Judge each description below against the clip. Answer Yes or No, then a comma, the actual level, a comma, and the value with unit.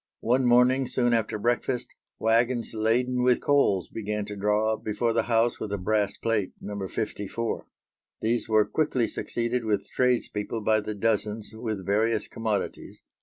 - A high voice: No, low, 110 Hz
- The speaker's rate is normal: Yes, average, 155 wpm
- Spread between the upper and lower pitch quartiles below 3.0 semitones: Yes, narrow, 2.4 semitones